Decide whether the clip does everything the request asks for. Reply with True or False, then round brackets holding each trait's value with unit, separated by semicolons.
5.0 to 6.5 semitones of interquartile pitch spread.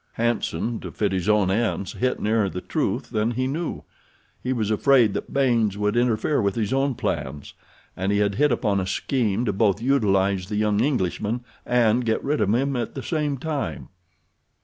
False (3.9 semitones)